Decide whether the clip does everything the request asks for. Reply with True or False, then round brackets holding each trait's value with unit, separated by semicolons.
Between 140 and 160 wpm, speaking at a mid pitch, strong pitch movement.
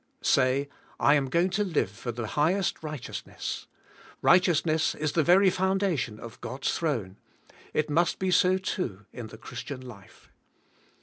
True (145 wpm; 155 Hz; 6.7 semitones)